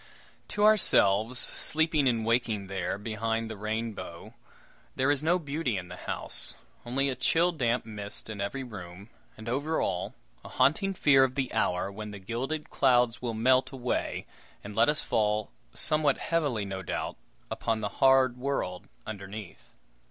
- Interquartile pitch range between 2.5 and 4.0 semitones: No, average, 4.7 semitones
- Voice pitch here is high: No, low, 115 Hz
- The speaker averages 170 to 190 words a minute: No, average, 160 wpm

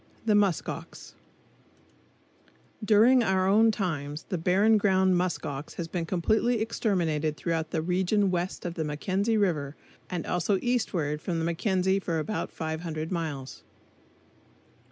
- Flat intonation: No, average, 4.0 semitones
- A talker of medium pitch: Yes, medium, 180 Hz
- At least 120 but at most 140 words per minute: Yes, slow, 135 wpm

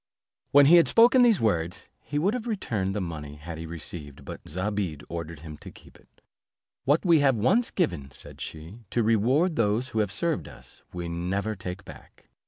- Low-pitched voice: Yes, low, 105 Hz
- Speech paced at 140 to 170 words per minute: No, average, 190 wpm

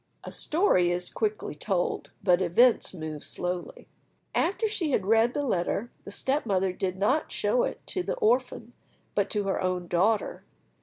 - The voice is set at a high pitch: Yes, high, 205 Hz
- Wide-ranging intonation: Yes, wide, 6.0 semitones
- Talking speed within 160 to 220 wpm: Yes, average, 165 wpm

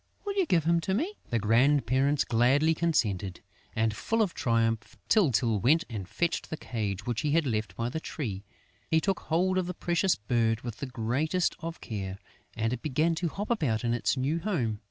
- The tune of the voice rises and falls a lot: Yes, wide, 6.8 semitones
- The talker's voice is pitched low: Yes, low, 130 Hz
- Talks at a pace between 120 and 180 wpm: No, average, 195 wpm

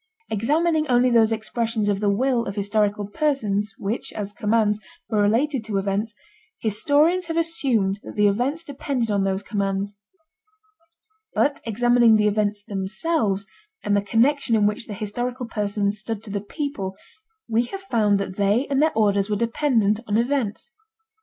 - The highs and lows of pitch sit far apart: No, average, 3.6 semitones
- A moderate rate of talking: Yes, average, 160 wpm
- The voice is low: No, high, 220 Hz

